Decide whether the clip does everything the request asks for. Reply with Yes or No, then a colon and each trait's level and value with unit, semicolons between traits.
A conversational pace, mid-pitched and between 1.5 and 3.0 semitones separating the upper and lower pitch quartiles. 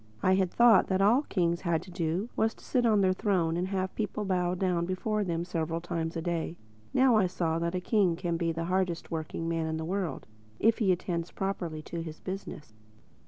No: fast, 215 wpm; medium, 180 Hz; narrow, 2.6 semitones